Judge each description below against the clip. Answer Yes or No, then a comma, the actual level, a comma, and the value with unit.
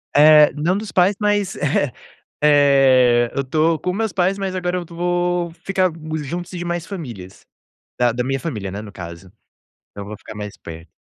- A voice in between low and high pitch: Yes, medium, 155 Hz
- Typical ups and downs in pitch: No, wide, 6.7 semitones